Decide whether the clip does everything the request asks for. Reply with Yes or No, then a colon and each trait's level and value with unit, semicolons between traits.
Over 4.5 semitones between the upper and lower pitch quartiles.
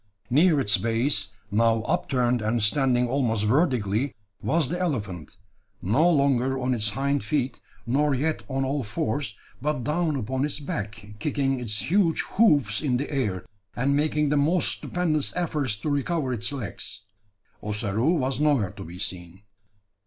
Yes: average, 5.3 semitones